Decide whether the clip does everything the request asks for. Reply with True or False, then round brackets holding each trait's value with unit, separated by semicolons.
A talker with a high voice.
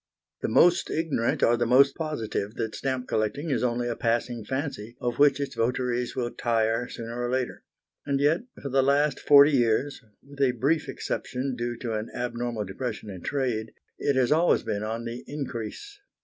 False (125 Hz)